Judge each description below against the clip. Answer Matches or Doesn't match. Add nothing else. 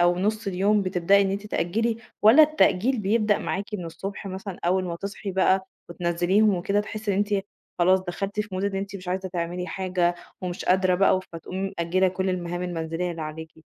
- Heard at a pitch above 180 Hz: Matches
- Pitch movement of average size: Doesn't match